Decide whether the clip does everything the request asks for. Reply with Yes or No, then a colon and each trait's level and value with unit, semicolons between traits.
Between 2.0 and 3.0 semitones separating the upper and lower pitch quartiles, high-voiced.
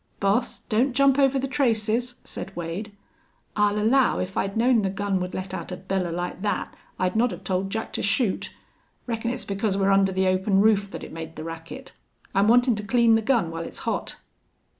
No: average, 3.7 semitones; high, 205 Hz